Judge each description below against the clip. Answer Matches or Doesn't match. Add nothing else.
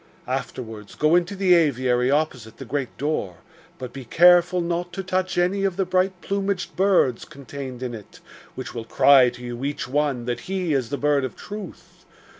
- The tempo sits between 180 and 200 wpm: Matches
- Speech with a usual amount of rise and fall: Doesn't match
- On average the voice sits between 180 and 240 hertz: Doesn't match